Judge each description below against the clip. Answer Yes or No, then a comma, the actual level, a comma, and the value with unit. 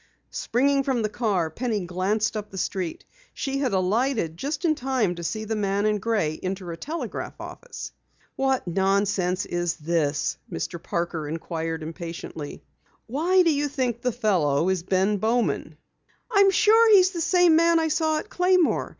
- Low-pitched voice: No, high, 215 Hz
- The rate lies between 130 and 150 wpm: No, average, 160 wpm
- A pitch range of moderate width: No, wide, 8.2 semitones